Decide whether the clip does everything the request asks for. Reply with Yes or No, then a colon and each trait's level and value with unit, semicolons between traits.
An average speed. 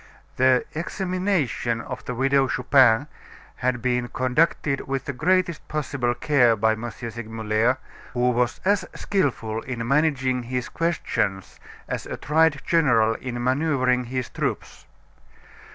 No: slow, 125 wpm